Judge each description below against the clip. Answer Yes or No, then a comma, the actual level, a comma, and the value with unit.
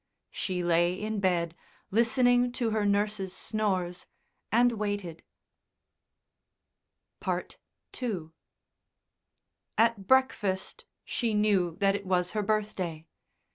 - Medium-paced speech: No, slow, 95 wpm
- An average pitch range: Yes, average, 3.3 semitones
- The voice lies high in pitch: Yes, high, 205 Hz